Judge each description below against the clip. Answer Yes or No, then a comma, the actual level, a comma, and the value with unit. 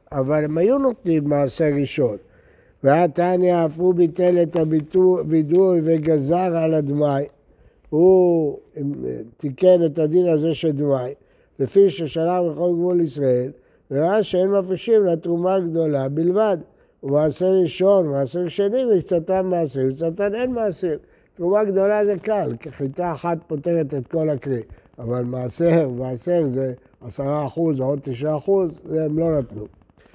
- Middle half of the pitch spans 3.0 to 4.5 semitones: Yes, average, 4.1 semitones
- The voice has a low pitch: No, medium, 165 Hz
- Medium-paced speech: Yes, average, 130 wpm